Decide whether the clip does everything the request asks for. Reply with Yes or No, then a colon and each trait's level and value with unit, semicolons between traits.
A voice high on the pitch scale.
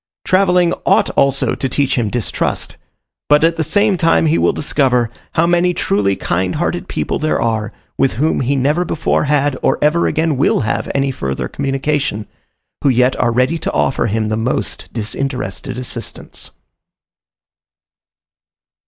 No: low, 135 Hz